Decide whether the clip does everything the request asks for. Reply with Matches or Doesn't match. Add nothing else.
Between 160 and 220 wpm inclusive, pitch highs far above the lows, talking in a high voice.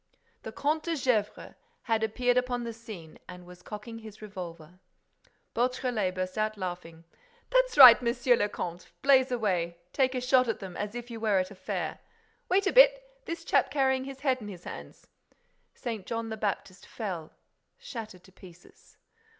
Matches